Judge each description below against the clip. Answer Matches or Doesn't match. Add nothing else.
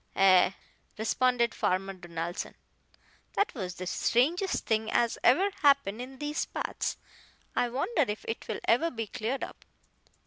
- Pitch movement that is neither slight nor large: Doesn't match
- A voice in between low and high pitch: Doesn't match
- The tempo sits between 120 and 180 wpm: Matches